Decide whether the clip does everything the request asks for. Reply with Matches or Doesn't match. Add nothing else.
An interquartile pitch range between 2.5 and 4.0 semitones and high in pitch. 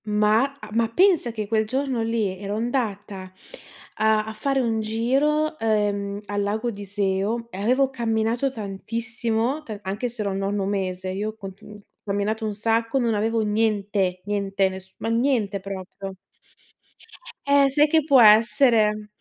Matches